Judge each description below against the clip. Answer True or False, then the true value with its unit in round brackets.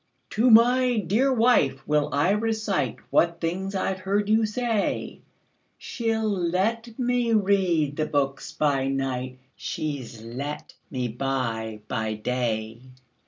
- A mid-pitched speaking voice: True (170 Hz)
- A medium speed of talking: False (120 wpm)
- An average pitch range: False (8.6 semitones)